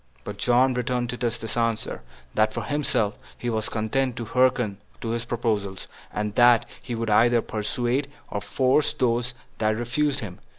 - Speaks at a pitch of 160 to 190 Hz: No, low, 120 Hz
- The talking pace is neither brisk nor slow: Yes, average, 165 wpm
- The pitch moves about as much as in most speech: No, narrow, 2.3 semitones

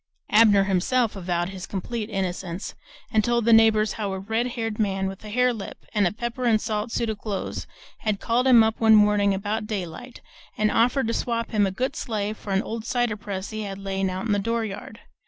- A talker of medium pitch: No, high, 215 Hz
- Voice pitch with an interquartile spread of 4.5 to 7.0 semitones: No, average, 2.7 semitones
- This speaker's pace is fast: Yes, fast, 215 wpm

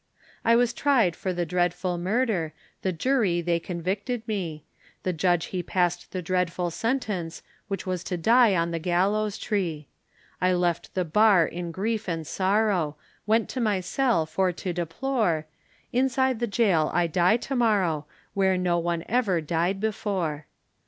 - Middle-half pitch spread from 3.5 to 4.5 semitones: Yes, average, 4.2 semitones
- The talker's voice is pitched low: No, medium, 185 Hz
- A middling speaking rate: Yes, average, 160 wpm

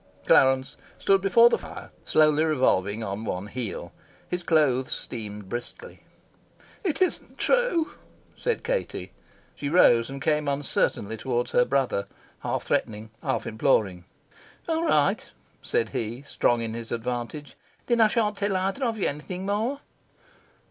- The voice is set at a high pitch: No, medium, 140 Hz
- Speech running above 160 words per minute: No, average, 140 wpm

